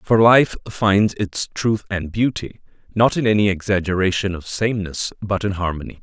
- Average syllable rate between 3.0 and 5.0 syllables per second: Yes, 4.9 syllables/s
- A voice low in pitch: Yes, low, 100 Hz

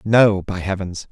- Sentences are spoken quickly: No, average, 160 wpm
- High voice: No, low, 100 Hz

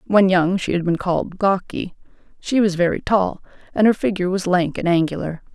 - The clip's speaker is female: Yes, female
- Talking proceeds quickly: No, average, 195 wpm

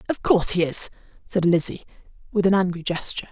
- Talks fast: No, average, 180 wpm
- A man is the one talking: No, female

